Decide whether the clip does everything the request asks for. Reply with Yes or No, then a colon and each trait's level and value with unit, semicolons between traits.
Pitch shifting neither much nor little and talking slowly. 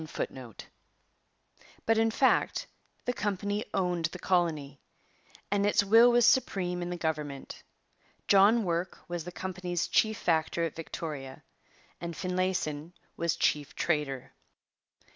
Yes: average, 4.0 semitones; slow, 120 wpm